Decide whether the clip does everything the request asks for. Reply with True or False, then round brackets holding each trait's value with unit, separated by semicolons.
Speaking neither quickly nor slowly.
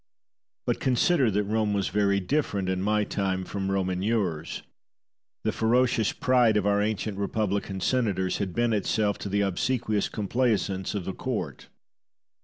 True (155 wpm)